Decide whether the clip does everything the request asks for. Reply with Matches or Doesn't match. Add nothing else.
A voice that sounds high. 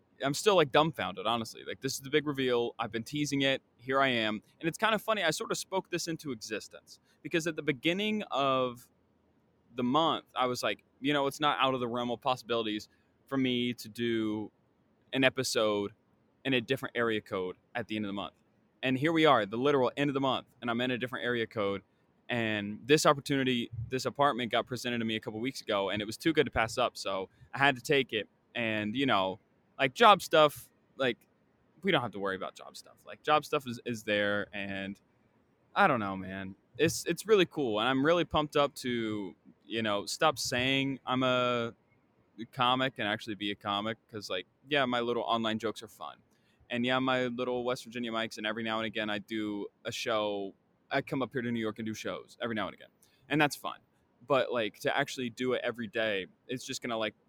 Doesn't match